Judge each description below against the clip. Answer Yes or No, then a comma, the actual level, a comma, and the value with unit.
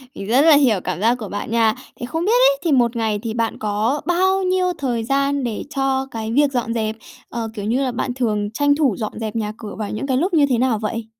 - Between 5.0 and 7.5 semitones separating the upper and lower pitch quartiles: No, average, 4.2 semitones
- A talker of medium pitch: No, high, 235 Hz